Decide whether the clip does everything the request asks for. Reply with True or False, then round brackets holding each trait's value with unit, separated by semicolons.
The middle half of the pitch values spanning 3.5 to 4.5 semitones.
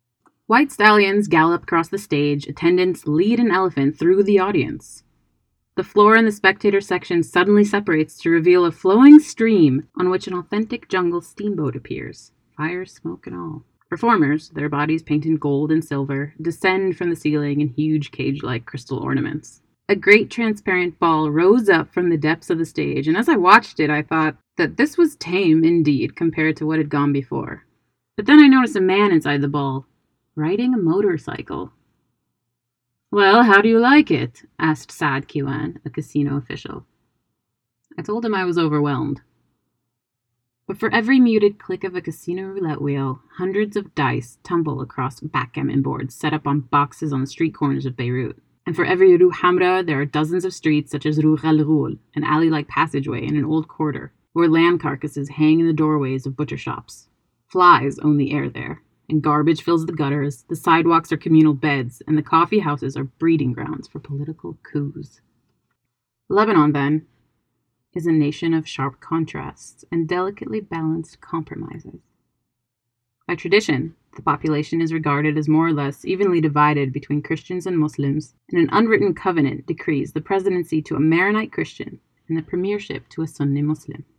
True (4.1 semitones)